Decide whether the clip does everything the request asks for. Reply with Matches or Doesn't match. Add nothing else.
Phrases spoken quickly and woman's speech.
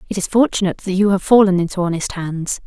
Matches